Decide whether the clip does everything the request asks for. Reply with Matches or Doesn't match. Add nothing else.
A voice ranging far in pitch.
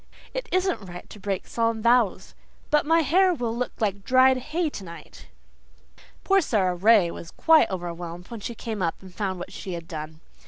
Matches